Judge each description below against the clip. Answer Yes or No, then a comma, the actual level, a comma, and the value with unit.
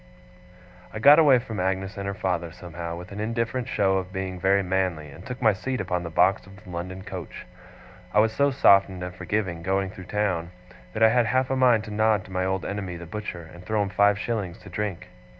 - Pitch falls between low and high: No, very low, 95 Hz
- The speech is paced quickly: Yes, fast, 230 wpm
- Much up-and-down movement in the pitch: No, average, 3.1 semitones